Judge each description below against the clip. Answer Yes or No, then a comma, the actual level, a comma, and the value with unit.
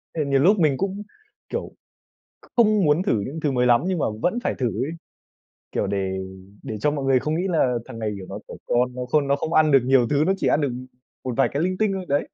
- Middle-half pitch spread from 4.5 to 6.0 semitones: Yes, wide, 5.5 semitones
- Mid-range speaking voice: Yes, medium, 145 Hz